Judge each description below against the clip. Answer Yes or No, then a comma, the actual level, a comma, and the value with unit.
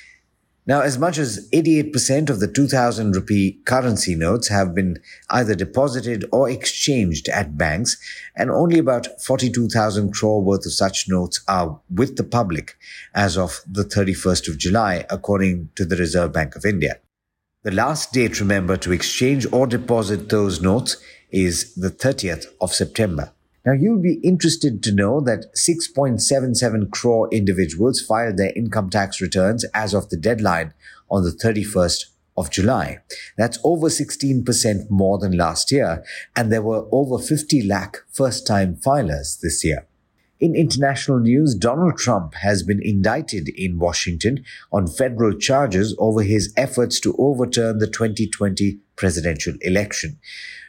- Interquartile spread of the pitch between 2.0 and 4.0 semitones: No, average, 5.1 semitones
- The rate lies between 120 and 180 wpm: Yes, average, 145 wpm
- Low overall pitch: Yes, low, 110 Hz